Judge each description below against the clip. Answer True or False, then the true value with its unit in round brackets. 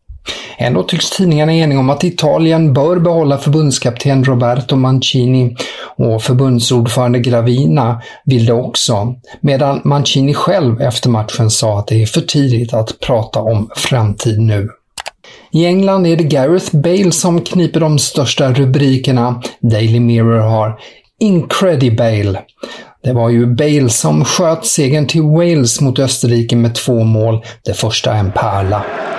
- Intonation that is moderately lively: True (4.5 semitones)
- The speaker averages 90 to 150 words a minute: True (140 wpm)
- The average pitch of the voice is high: False (130 Hz)